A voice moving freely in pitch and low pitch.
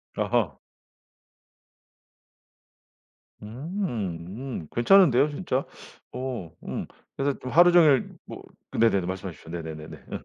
Yes: wide, 7.7 semitones; low, 125 Hz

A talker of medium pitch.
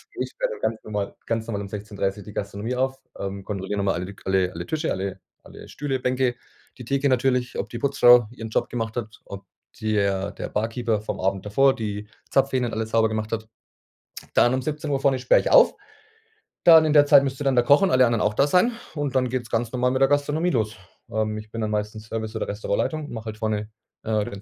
No: low, 115 Hz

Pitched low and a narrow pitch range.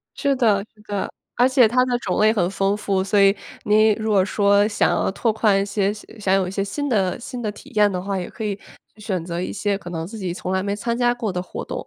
No: high, 205 Hz; narrow, 2.2 semitones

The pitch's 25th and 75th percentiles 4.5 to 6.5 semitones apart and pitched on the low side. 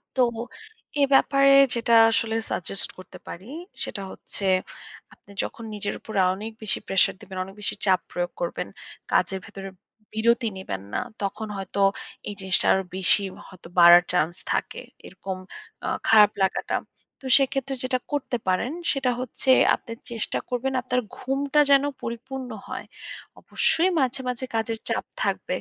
No: average, 5.2 semitones; high, 225 Hz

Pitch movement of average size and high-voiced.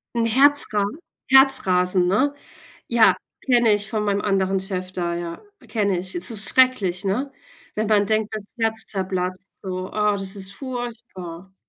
Yes: average, 3.4 semitones; high, 200 Hz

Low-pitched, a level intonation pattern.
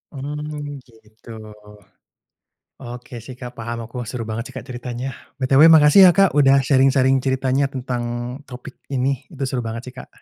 Yes: low, 130 Hz; narrow, 2.2 semitones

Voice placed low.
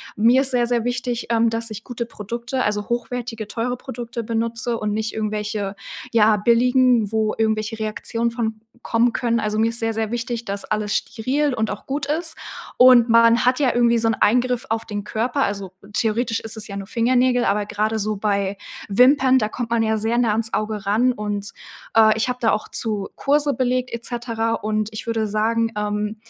No: high, 225 Hz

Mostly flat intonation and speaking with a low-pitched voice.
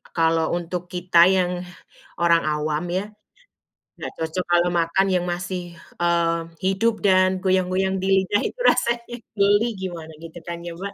No: narrow, 2.0 semitones; medium, 180 Hz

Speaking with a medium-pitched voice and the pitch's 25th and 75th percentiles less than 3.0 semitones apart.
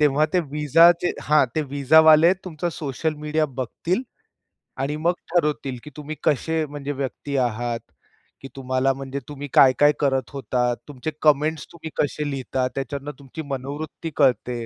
Yes: medium, 145 Hz; narrow, 2.5 semitones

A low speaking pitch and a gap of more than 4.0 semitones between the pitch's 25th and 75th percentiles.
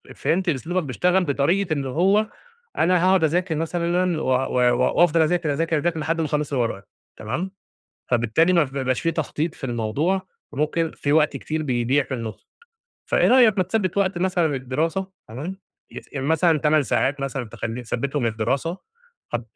No: medium, 155 Hz; average, 4.9 semitones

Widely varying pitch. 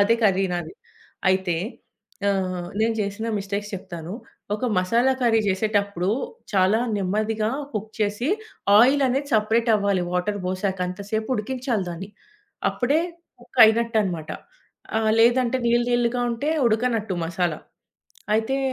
No: average, 3.6 semitones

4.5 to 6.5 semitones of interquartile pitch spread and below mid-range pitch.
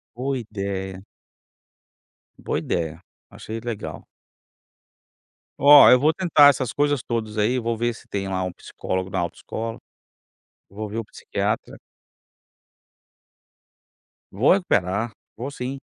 Yes: average, 4.8 semitones; low, 115 Hz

